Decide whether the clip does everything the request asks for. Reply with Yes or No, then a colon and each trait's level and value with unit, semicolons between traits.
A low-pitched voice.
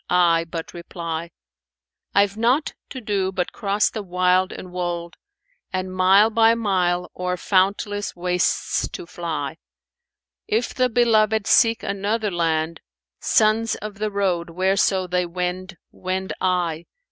No: medium, 185 Hz